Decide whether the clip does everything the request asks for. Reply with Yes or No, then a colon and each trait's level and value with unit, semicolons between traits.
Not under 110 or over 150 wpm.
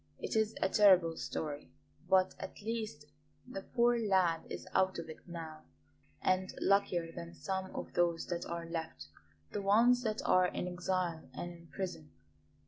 No: average, 160 wpm